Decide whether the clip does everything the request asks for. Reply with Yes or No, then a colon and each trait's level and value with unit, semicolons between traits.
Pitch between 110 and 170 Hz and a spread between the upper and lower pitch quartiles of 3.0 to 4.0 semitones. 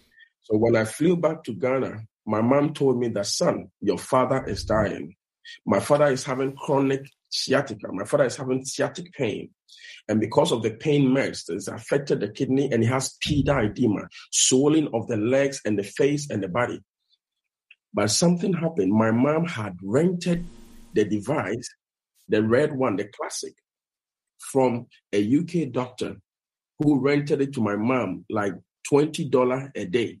No: low, 135 Hz; average, 5.1 semitones